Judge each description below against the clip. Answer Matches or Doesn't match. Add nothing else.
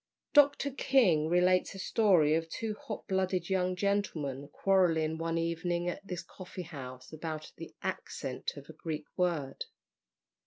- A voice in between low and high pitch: Matches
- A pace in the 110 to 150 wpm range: Matches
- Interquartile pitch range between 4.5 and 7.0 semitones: Doesn't match